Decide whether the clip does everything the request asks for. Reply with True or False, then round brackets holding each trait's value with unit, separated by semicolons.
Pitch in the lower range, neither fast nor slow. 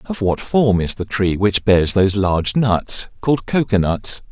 True (105 Hz; 195 wpm)